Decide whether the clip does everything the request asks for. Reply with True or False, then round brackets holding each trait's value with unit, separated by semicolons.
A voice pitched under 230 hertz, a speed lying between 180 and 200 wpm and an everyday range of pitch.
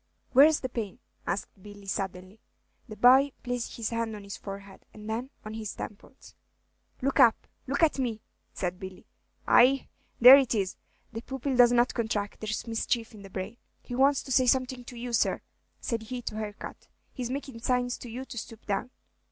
False (235 Hz; 185 wpm; 3.3 semitones)